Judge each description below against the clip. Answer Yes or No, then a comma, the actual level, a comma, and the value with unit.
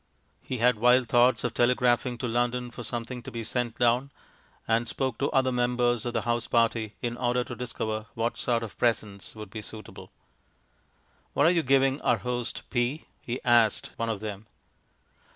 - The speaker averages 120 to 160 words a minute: No, average, 180 wpm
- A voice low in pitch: Yes, low, 120 Hz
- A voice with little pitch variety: Yes, narrow, 1.5 semitones